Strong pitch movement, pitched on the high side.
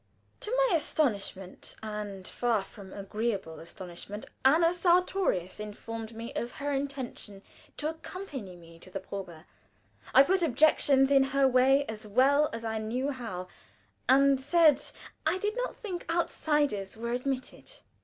Yes: wide, 6.3 semitones; very high, 255 Hz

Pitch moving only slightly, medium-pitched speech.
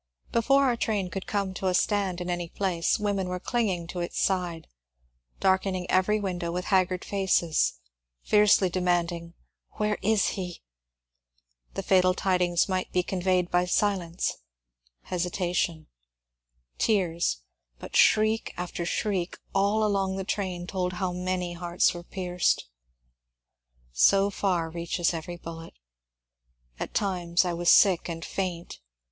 Yes: narrow, 2.1 semitones; medium, 180 Hz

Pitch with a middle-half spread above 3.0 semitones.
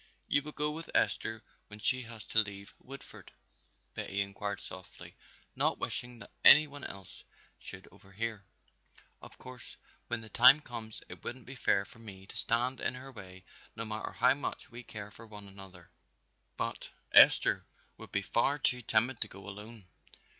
Yes: average, 4.0 semitones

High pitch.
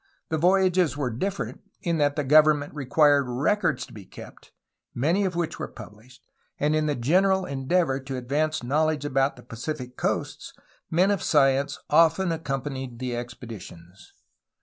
No: medium, 145 Hz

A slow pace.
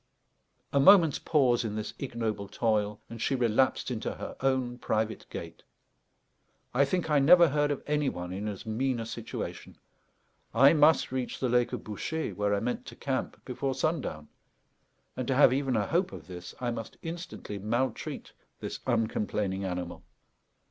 No: average, 165 wpm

